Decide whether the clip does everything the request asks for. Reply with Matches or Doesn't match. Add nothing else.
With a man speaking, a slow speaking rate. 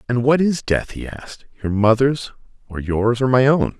Doesn't match